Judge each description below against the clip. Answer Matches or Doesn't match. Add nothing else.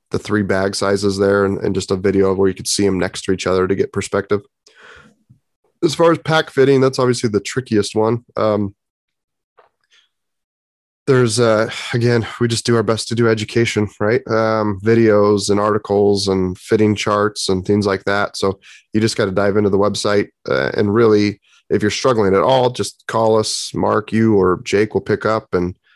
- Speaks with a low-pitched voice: Matches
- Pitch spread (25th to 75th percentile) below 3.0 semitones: Matches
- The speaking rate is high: Doesn't match